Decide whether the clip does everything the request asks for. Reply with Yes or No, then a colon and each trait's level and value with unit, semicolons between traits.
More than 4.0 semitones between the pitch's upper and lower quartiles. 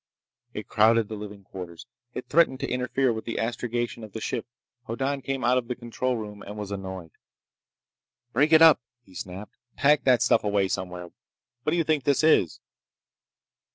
Yes: average, 4.4 semitones